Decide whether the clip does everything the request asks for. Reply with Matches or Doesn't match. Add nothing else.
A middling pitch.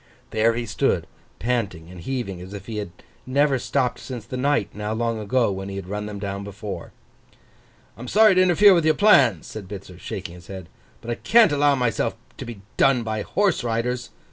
Doesn't match